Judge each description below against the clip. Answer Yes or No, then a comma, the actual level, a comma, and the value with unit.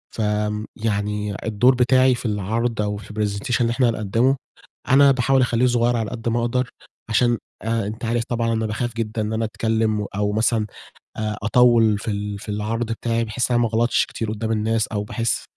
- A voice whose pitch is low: Yes, low, 115 Hz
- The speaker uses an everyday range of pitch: No, narrow, 2.0 semitones